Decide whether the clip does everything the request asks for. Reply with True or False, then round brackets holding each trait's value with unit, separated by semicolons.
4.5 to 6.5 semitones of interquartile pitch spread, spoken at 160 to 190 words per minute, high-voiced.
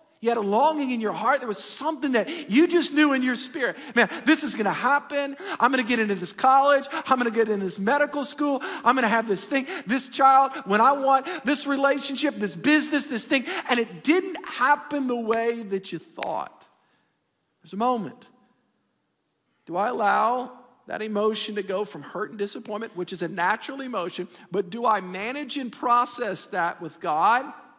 False (5.1 semitones; 200 wpm; 250 Hz)